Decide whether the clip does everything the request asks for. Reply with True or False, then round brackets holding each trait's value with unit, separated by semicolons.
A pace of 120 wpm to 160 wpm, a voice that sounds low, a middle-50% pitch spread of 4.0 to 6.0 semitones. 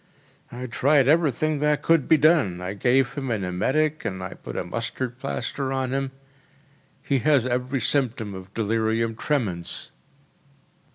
True (145 wpm; 125 Hz; 4.5 semitones)